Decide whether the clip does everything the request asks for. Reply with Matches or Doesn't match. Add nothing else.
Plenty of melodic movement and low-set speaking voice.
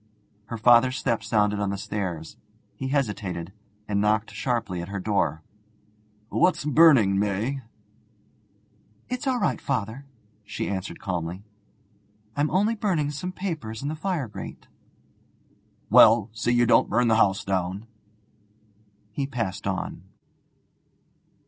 Matches